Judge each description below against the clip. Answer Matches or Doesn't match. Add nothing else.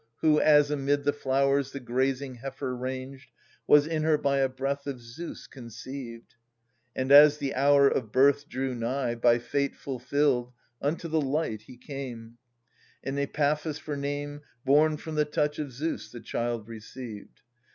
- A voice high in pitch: Doesn't match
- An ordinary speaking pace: Matches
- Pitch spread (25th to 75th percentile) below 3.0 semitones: Matches